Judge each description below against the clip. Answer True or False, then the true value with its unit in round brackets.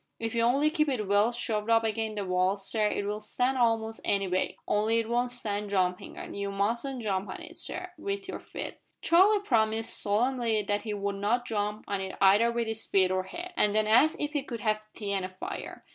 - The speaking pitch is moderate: False (220 Hz)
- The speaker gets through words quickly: True (220 wpm)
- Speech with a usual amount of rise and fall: True (3.2 semitones)